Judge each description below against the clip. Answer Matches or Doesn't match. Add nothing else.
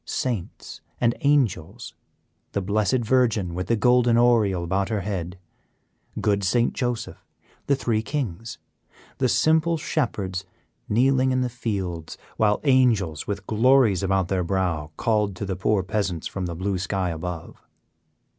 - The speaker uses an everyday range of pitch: Matches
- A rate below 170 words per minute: Matches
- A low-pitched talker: Matches